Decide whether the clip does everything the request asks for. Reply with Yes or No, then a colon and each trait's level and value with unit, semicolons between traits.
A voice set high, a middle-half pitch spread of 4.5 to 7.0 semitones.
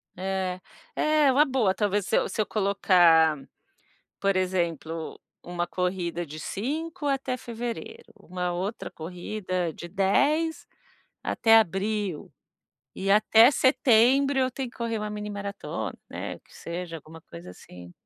Yes: high, 195 Hz; average, 5.2 semitones